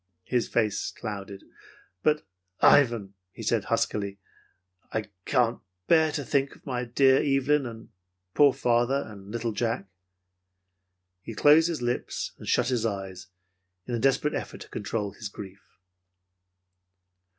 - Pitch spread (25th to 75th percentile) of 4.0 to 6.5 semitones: Yes, average, 4.7 semitones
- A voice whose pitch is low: Yes, low, 120 Hz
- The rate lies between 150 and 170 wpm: No, slow, 135 wpm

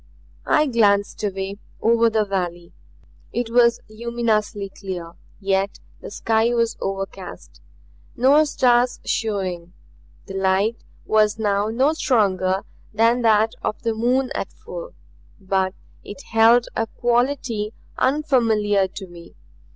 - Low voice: No, high, 215 Hz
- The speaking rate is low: Yes, slow, 115 wpm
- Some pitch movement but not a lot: Yes, average, 3.4 semitones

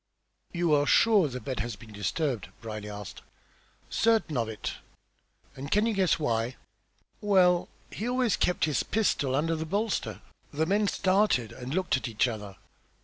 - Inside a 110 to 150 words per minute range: No, average, 160 wpm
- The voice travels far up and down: Yes, wide, 8.7 semitones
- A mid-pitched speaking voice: Yes, medium, 150 Hz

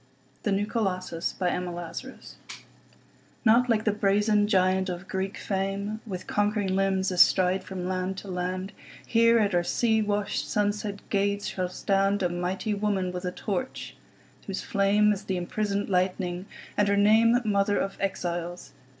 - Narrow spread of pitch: Yes, narrow, 2.1 semitones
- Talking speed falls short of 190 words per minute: Yes, slow, 135 wpm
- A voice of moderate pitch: No, high, 195 Hz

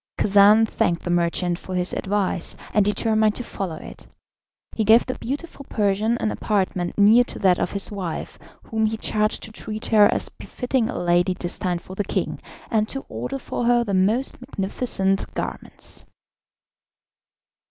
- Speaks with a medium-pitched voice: No, high, 210 Hz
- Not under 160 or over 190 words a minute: Yes, average, 165 wpm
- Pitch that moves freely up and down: No, average, 3.1 semitones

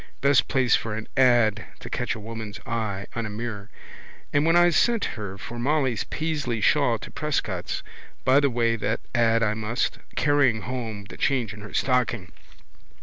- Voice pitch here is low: Yes, low, 115 Hz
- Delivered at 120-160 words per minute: No, average, 175 wpm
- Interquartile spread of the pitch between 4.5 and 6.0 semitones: No, average, 3.6 semitones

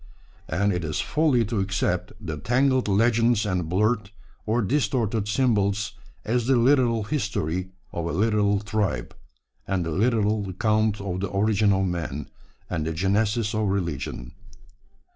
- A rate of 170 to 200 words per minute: No, average, 145 wpm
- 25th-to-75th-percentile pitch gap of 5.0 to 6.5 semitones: No, average, 3.4 semitones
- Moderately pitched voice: No, low, 105 Hz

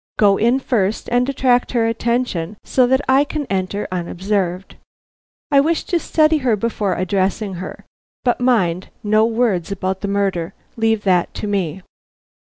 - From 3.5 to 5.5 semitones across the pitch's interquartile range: Yes, average, 4.6 semitones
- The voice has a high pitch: Yes, high, 210 Hz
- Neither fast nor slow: Yes, average, 155 wpm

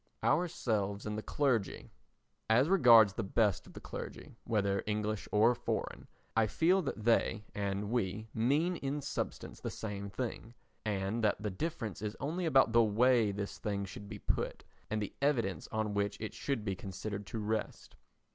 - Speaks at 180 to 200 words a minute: No, average, 170 wpm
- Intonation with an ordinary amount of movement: Yes, average, 3.3 semitones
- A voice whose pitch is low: Yes, low, 110 Hz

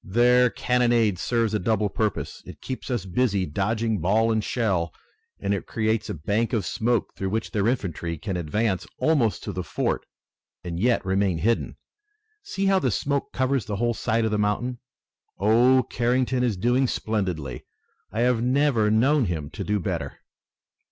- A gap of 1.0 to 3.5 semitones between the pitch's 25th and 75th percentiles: No, average, 4.1 semitones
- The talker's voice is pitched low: Yes, low, 110 Hz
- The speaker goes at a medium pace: Yes, average, 170 wpm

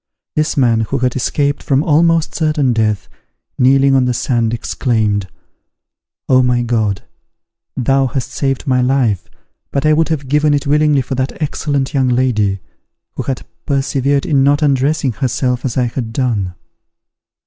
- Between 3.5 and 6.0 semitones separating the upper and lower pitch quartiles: No, average, 2.8 semitones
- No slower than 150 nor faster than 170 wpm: Yes, average, 155 wpm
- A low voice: Yes, low, 130 Hz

